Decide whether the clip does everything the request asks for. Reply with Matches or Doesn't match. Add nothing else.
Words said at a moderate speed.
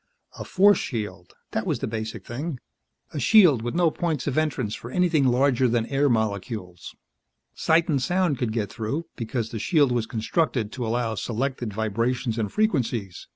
Matches